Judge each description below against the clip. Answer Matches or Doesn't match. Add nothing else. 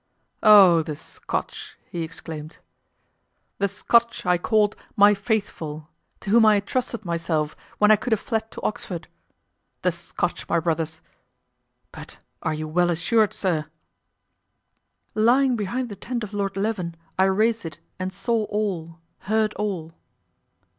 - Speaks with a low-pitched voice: Doesn't match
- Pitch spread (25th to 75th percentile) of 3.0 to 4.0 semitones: Doesn't match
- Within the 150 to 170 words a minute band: Doesn't match